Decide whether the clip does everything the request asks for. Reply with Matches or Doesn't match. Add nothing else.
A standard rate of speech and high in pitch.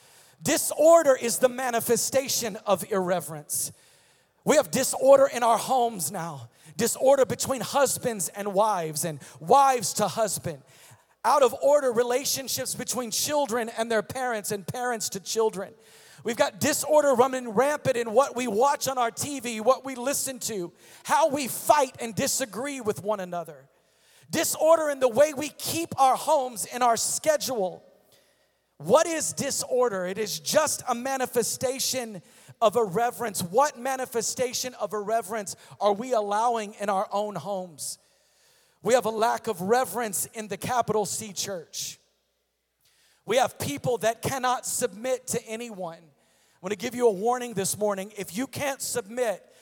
Matches